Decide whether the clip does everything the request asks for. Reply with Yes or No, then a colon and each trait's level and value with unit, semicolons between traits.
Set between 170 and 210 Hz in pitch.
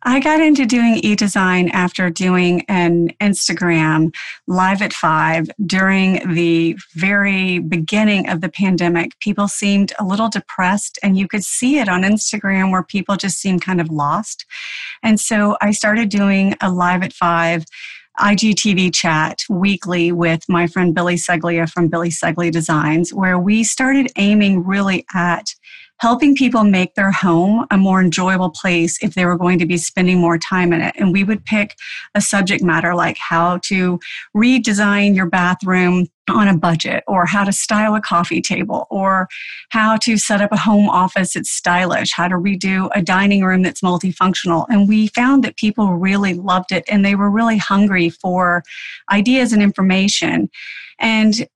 Yes: high, 190 Hz